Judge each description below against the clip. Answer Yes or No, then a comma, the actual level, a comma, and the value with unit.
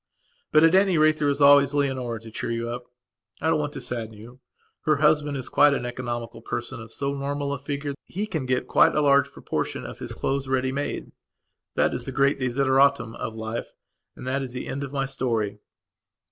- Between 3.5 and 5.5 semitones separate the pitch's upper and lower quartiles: No, average, 2.8 semitones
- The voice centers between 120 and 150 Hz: Yes, low, 135 Hz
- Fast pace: Yes, fast, 215 wpm